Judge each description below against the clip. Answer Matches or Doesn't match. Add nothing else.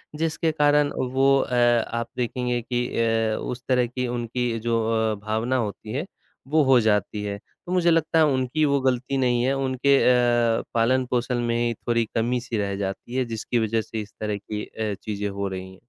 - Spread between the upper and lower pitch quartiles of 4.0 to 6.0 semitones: Doesn't match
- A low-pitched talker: Matches